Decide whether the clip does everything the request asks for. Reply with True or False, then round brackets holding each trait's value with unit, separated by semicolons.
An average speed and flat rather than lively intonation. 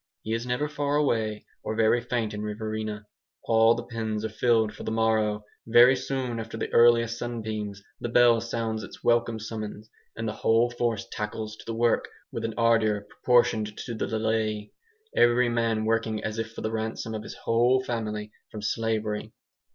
True (180 wpm; 1.5 semitones)